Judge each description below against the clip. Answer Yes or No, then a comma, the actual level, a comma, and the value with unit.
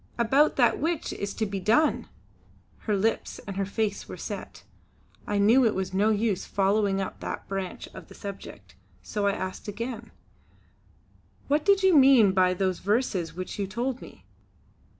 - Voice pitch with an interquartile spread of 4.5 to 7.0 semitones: No, average, 3.6 semitones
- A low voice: No, high, 205 Hz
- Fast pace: No, average, 170 wpm